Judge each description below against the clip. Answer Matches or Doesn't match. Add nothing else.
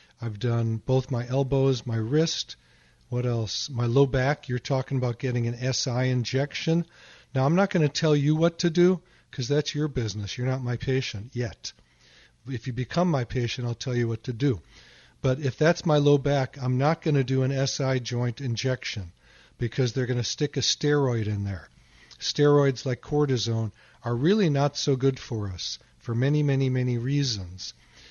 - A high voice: Doesn't match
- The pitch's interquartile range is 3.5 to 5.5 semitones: Doesn't match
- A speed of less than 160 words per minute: Doesn't match